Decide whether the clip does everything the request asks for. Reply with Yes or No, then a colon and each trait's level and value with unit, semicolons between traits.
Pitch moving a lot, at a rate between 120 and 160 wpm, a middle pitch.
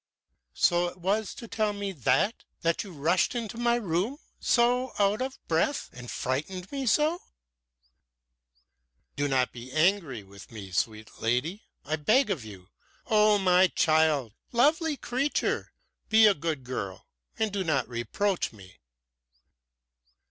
Yes: wide, 8.8 semitones; average, 140 wpm; medium, 180 Hz